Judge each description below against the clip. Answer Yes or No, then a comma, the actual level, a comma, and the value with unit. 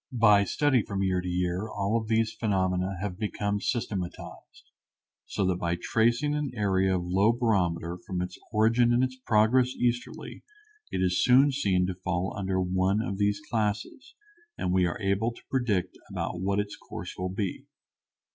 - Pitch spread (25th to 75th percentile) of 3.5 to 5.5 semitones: Yes, average, 3.8 semitones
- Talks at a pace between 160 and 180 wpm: Yes, average, 170 wpm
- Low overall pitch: Yes, low, 100 Hz